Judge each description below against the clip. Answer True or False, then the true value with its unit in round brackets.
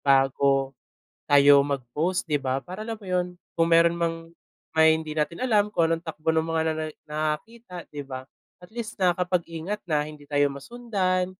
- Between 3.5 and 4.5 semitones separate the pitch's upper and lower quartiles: True (4.1 semitones)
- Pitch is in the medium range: True (165 Hz)